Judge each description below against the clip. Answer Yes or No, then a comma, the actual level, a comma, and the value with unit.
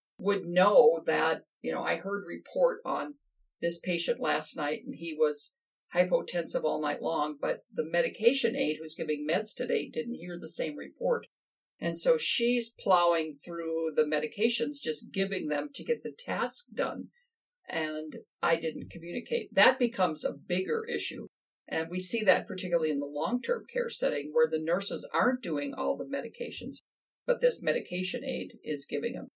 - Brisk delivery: No, average, 170 wpm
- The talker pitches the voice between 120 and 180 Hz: No, high, 200 Hz